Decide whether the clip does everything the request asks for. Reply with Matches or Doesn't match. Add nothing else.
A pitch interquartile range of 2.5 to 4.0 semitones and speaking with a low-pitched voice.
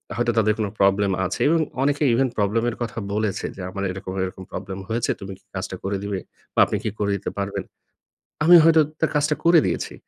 Doesn't match